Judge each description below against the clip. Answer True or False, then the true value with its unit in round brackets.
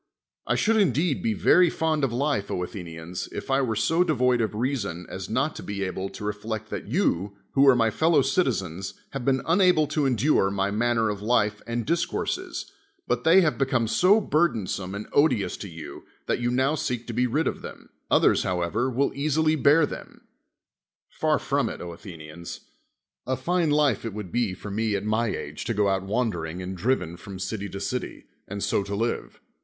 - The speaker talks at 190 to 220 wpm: True (195 wpm)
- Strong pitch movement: True (6.0 semitones)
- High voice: False (115 Hz)